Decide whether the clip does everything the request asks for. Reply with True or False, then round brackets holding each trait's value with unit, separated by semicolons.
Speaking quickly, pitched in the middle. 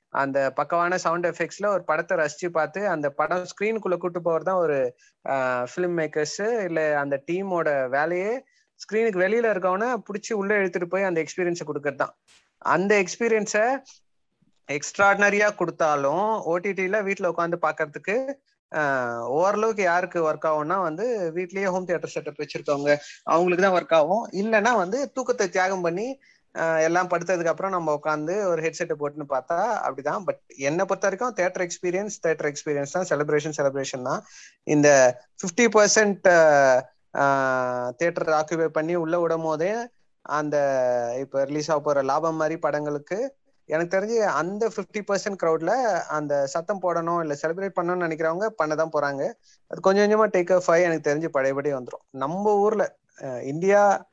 True (140 wpm; 170 Hz)